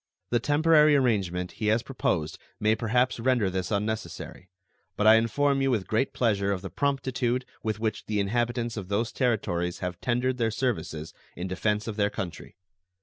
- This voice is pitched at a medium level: No, low, 110 Hz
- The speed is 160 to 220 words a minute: Yes, average, 170 wpm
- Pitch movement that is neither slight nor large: Yes, average, 4.0 semitones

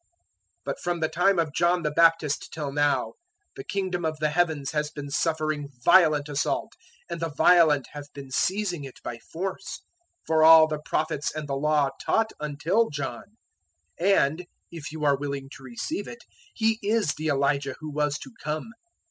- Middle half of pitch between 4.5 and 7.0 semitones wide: No, average, 3.2 semitones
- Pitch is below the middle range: No, medium, 155 Hz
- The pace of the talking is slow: No, average, 180 wpm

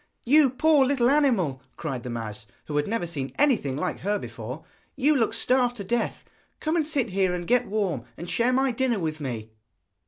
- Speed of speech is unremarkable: Yes, average, 195 wpm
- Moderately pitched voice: No, high, 210 Hz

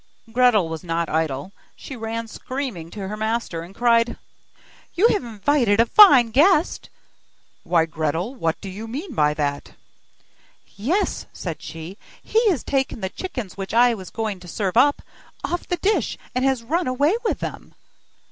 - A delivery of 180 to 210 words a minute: No, average, 165 wpm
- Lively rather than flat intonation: Yes, wide, 7.0 semitones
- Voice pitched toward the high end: Yes, high, 225 Hz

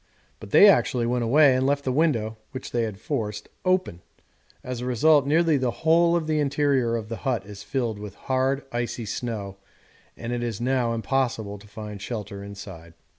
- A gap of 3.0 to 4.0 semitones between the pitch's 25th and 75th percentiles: No, average, 4.6 semitones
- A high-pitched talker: No, low, 120 Hz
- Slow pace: No, average, 185 wpm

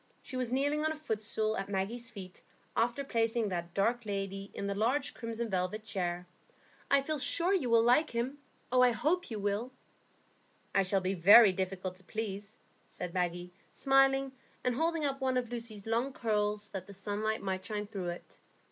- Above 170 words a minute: Yes, average, 180 wpm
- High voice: Yes, high, 220 Hz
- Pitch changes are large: No, average, 4.3 semitones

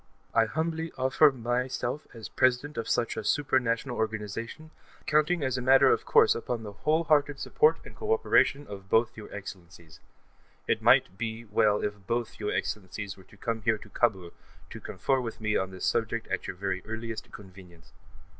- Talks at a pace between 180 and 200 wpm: Yes, average, 185 wpm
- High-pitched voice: No, low, 115 Hz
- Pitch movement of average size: Yes, average, 4.3 semitones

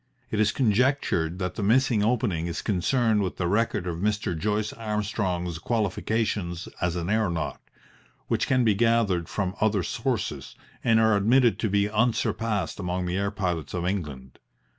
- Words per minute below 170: Yes, average, 160 wpm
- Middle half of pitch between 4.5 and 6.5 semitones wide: No, average, 3.9 semitones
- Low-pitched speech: Yes, low, 100 Hz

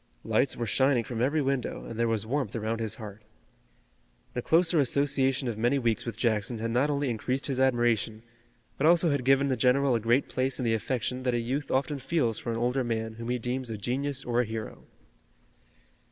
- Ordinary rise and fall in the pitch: Yes, average, 3.0 semitones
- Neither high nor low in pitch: No, low, 125 Hz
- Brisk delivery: Yes, fast, 210 wpm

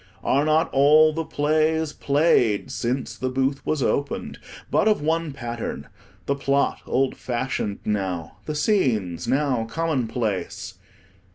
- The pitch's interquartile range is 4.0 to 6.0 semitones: Yes, average, 4.6 semitones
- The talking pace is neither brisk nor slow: No, slow, 125 wpm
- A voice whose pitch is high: No, medium, 140 Hz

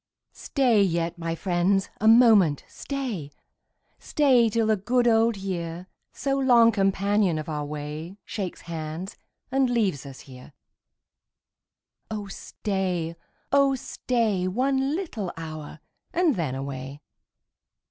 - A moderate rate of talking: No, slow, 120 wpm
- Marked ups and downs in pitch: Yes, wide, 6.2 semitones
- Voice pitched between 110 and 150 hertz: No, high, 195 Hz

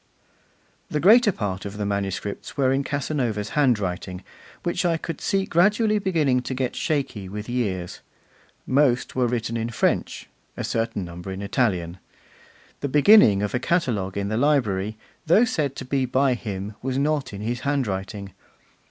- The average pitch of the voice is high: No, low, 125 Hz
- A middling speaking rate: Yes, average, 160 wpm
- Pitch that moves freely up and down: Yes, wide, 6.2 semitones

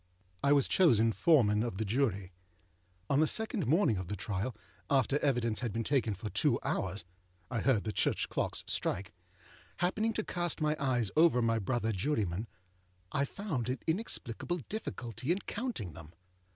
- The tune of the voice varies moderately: No, wide, 6.6 semitones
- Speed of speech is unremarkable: Yes, average, 165 wpm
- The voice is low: Yes, low, 120 Hz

